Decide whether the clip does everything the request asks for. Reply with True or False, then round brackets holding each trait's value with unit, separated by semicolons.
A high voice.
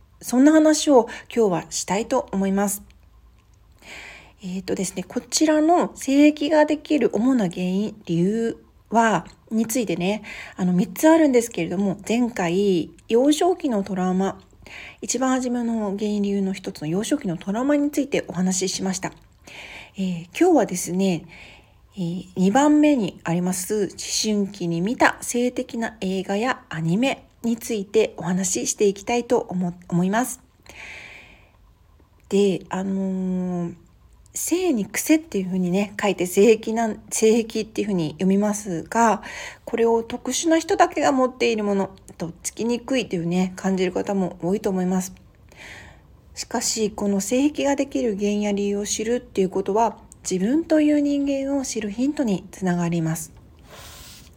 True (205 Hz)